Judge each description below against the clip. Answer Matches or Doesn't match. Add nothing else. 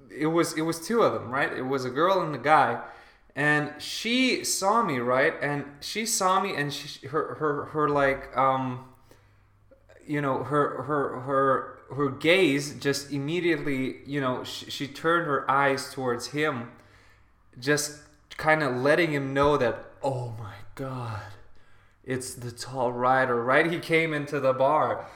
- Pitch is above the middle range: Doesn't match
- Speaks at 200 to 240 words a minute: Doesn't match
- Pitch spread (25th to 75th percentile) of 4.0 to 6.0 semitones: Doesn't match